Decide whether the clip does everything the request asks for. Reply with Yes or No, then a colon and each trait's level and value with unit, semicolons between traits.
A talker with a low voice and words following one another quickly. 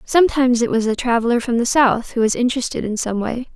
No: high, 240 Hz; fast, 235 wpm